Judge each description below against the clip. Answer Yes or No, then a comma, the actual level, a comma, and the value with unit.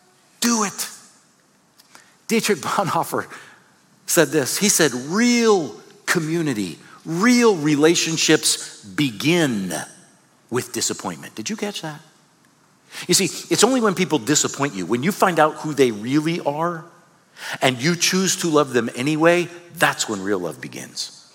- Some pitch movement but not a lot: Yes, average, 3.8 semitones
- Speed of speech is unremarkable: No, slow, 130 wpm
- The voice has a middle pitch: Yes, medium, 170 Hz